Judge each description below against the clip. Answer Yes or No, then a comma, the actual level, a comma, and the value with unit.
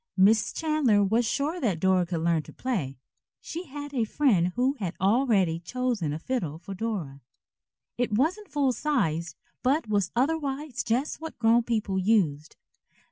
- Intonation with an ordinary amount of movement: No, wide, 6.8 semitones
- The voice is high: Yes, high, 225 Hz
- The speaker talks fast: No, average, 155 wpm